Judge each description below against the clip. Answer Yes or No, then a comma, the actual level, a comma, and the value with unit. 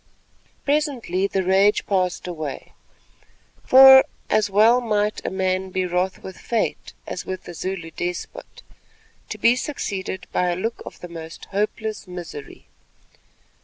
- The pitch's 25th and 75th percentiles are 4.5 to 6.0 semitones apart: No, average, 3.5 semitones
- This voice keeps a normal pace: No, slow, 130 wpm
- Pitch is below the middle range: No, high, 190 Hz